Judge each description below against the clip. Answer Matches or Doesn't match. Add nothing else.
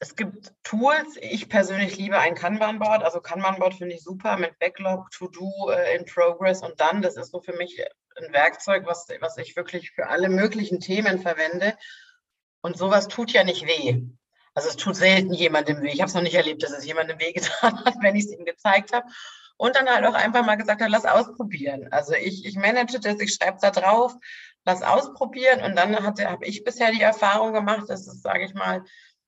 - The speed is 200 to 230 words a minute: Matches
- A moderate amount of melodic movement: Matches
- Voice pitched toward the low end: Doesn't match